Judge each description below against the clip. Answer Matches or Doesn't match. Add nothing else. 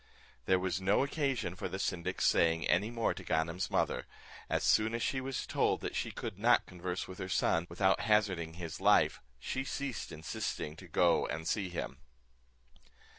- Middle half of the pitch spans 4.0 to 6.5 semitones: Matches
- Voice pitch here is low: Matches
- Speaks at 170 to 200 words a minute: Matches